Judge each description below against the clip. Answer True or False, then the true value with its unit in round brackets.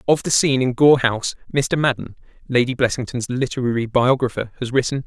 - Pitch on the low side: True (125 Hz)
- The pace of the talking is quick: False (165 wpm)